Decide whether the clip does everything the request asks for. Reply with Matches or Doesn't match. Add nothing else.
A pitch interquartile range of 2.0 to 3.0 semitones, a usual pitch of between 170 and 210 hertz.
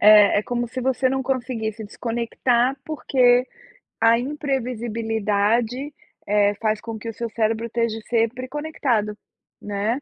Doesn't match